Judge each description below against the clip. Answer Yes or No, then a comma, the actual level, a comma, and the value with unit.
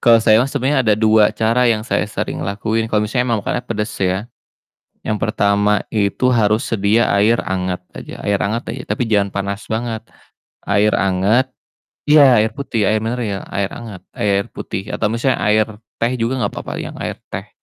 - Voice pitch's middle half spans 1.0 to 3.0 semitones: Yes, narrow, 2.5 semitones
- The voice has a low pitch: Yes, low, 110 Hz